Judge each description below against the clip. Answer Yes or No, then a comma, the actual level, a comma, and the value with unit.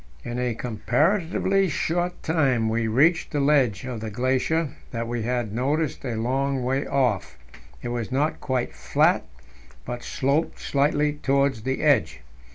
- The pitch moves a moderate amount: Yes, average, 3.7 semitones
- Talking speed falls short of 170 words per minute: Yes, average, 150 wpm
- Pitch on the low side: Yes, low, 130 Hz